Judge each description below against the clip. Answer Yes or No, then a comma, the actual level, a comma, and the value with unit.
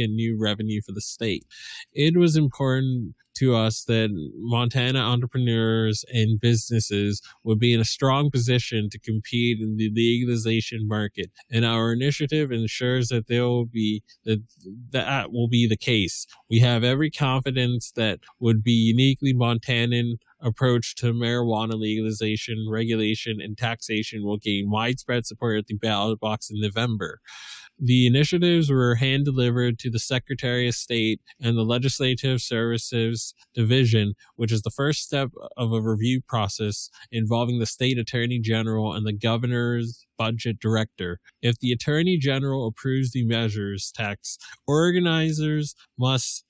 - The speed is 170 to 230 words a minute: No, average, 145 wpm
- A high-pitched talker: No, low, 115 Hz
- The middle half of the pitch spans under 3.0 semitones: Yes, narrow, 2.4 semitones